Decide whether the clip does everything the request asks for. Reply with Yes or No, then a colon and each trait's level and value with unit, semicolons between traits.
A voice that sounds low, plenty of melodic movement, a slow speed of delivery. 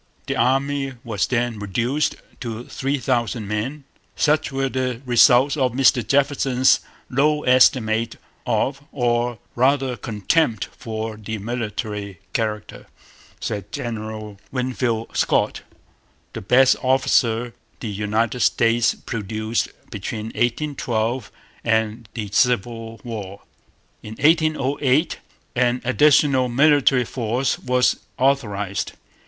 No: low, 120 Hz; average, 3.3 semitones; slow, 105 wpm